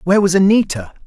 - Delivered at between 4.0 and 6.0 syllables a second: No, 6.9 syllables/s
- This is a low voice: No, medium, 185 Hz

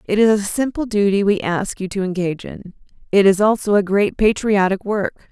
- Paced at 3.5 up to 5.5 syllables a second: Yes, 5.3 syllables/s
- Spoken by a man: No, female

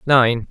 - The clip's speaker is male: Yes, male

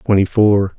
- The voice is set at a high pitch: No, low, 100 Hz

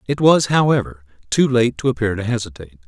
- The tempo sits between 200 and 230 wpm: No, average, 190 wpm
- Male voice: Yes, male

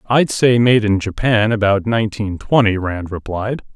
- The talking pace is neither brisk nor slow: Yes, average, 160 wpm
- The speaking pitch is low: Yes, low, 110 Hz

